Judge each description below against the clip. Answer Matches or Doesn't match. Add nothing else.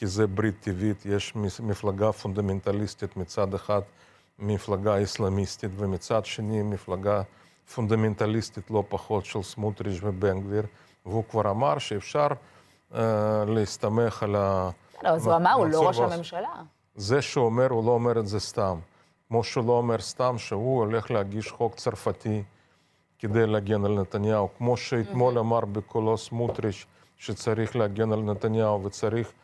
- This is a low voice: Matches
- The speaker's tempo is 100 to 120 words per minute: Doesn't match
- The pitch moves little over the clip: Matches